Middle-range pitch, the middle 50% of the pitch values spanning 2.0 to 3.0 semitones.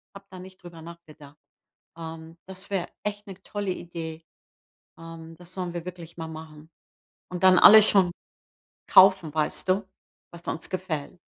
Yes: medium, 175 Hz; narrow, 2.5 semitones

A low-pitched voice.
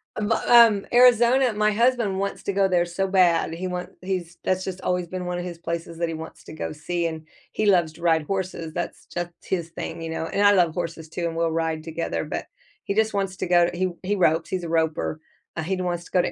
No: medium, 180 Hz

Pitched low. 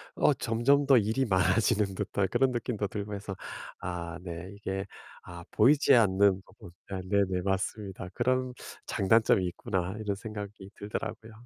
Yes: low, 100 Hz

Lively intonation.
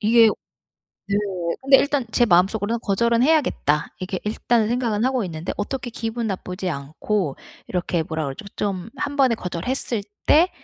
No: average, 5.0 semitones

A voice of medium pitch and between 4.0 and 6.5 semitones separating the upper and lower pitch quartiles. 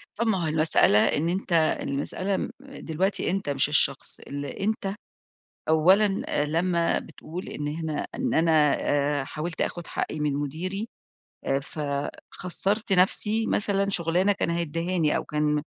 Yes: medium, 170 Hz; average, 4.5 semitones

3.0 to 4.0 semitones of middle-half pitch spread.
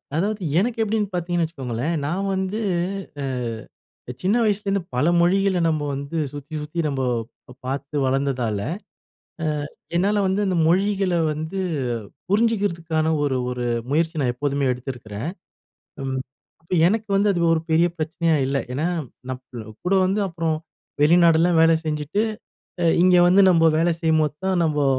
No: average, 4.9 semitones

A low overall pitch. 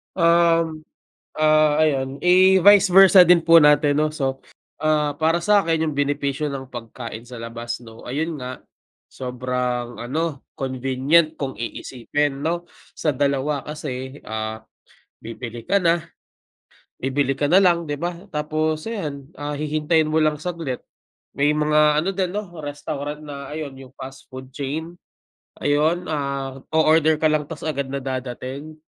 No: medium, 150 Hz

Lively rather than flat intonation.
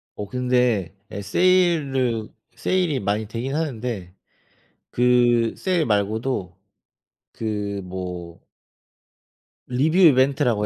No: average, 4.8 semitones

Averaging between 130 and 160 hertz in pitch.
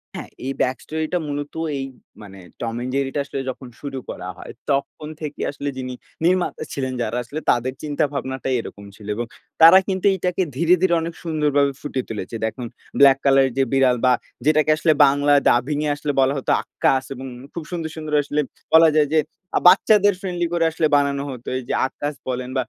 Yes: medium, 140 Hz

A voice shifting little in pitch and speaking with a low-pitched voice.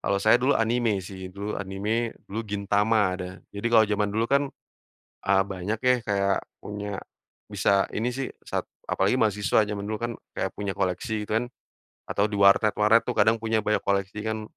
Yes: narrow, 2.0 semitones; low, 105 Hz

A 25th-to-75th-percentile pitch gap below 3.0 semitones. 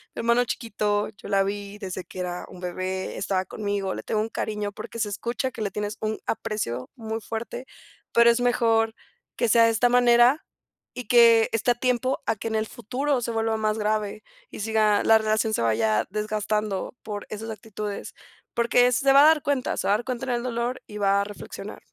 Yes: narrow, 2.5 semitones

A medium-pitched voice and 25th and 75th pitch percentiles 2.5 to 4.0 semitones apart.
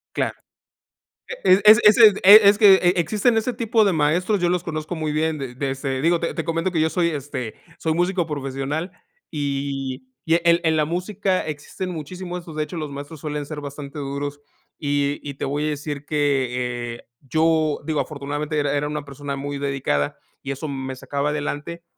Yes: medium, 150 Hz; average, 3.3 semitones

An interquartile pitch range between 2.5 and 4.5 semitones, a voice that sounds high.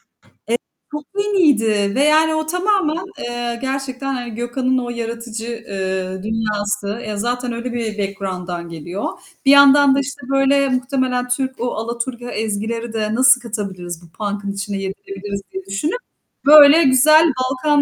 No: average, 4.9 semitones; high, 240 Hz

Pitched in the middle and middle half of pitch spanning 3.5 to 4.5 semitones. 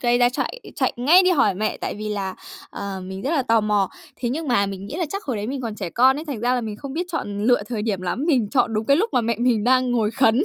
No: high, 240 Hz; average, 4.2 semitones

